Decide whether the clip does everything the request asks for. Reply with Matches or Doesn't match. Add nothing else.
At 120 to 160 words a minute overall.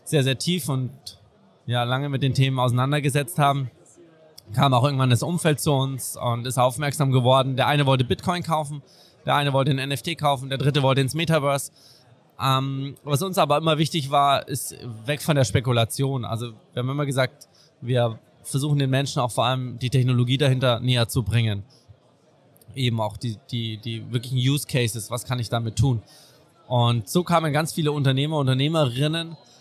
Doesn't match